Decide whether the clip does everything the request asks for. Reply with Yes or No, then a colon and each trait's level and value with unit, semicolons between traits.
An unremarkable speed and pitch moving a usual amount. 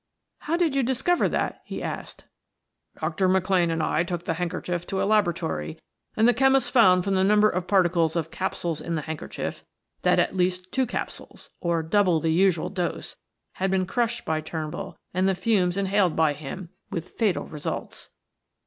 Yes: average, 175 wpm; average, 3.6 semitones